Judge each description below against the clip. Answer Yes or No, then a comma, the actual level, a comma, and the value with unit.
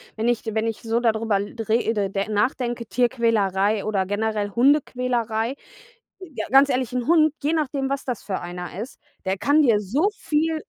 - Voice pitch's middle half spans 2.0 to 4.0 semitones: No, average, 4.4 semitones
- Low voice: No, high, 230 Hz